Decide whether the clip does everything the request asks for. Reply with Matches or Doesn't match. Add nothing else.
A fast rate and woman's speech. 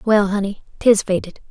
Doesn't match